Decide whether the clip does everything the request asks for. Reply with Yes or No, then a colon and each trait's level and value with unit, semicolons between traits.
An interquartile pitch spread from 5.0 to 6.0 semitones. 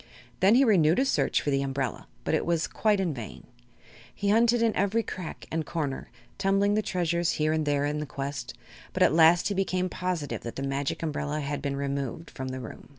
Yes: wide, 5.4 semitones